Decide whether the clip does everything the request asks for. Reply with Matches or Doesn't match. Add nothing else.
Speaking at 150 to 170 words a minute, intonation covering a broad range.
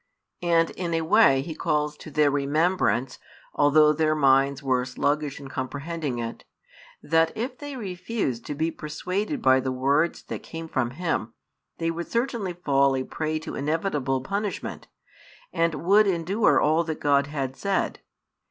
Doesn't match